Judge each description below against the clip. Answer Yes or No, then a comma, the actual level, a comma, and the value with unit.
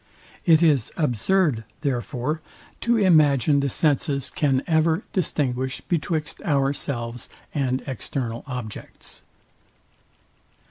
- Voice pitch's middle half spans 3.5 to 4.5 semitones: Yes, average, 3.8 semitones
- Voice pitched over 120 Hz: Yes, medium, 140 Hz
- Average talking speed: No, slow, 90 wpm